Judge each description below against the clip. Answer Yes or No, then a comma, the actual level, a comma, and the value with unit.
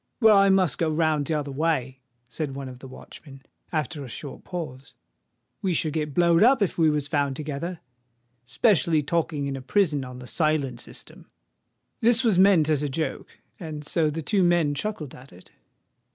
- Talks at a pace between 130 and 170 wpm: No, average, 180 wpm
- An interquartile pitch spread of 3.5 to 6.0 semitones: Yes, average, 4.0 semitones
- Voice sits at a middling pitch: Yes, medium, 150 Hz